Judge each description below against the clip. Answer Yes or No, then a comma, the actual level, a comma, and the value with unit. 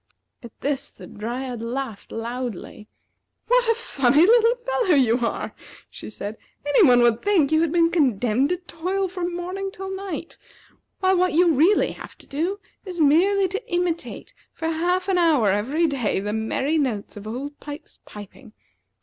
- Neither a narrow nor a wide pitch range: No, wide, 7.1 semitones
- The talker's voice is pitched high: Yes, very high, 315 Hz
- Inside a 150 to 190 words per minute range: Yes, average, 165 wpm